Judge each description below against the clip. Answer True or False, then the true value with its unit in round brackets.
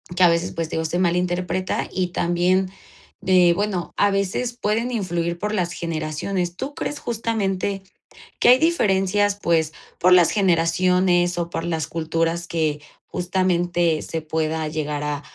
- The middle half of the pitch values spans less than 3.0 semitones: True (2.5 semitones)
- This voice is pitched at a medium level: True (175 Hz)